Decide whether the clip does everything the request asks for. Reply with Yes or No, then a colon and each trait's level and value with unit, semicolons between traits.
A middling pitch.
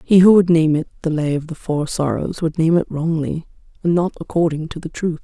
Yes: medium, 160 Hz